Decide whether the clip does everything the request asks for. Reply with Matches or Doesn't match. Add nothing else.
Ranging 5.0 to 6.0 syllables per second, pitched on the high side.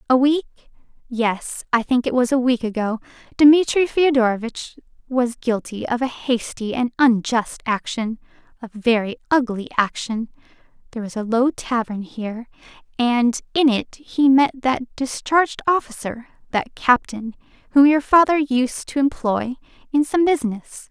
Doesn't match